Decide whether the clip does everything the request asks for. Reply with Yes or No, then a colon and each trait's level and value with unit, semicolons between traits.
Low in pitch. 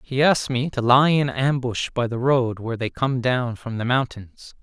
Yes: low, 125 Hz